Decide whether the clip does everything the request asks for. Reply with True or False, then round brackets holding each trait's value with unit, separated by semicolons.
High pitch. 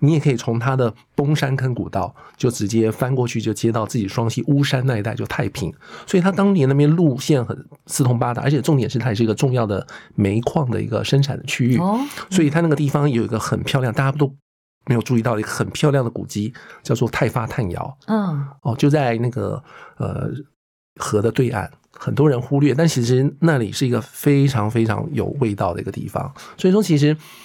False (130 Hz)